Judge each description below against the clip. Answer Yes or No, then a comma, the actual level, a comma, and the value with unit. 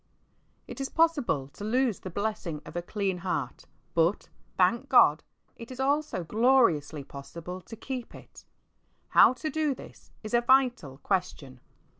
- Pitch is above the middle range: Yes, high, 210 Hz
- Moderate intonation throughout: No, wide, 7.5 semitones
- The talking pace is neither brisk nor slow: Yes, average, 155 wpm